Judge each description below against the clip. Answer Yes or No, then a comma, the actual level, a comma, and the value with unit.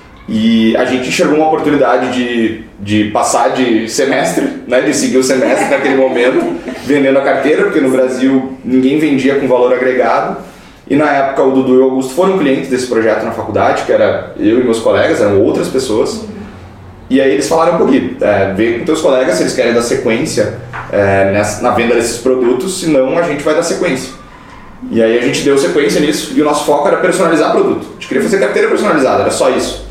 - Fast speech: Yes, fast, 205 wpm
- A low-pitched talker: Yes, low, 130 Hz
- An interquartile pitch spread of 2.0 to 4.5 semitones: Yes, average, 3.4 semitones